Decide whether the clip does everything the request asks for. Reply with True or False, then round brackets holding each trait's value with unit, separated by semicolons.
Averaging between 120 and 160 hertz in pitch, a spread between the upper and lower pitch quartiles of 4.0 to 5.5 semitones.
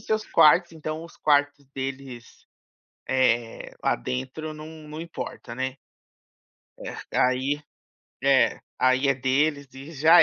False (140 Hz; 3.0 semitones)